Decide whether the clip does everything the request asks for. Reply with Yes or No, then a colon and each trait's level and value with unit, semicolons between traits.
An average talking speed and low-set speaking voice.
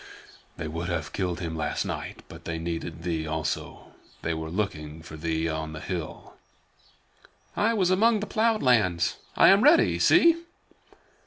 Yes: average, 160 wpm; very low, 85 Hz